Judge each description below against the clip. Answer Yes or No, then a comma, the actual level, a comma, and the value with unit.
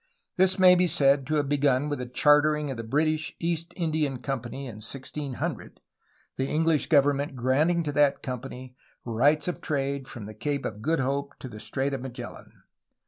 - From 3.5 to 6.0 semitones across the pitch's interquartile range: No, average, 2.9 semitones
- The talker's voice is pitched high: No, medium, 140 Hz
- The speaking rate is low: No, average, 180 wpm